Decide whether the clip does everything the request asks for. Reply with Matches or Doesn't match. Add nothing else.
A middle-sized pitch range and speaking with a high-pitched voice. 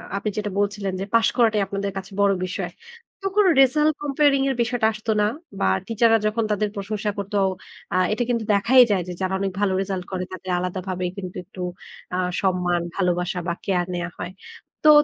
Matches